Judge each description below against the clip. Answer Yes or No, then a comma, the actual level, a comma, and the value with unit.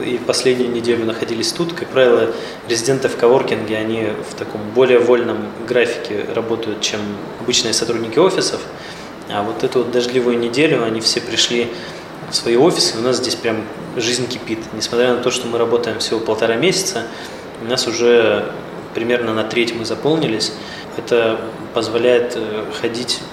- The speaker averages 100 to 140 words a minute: No, average, 155 wpm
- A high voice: No, low, 120 Hz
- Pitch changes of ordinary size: No, narrow, 1.6 semitones